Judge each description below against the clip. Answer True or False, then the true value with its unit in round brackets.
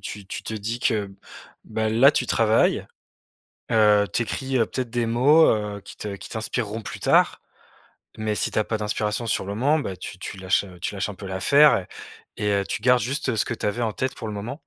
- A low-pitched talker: True (110 Hz)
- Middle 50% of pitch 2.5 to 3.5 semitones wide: True (2.9 semitones)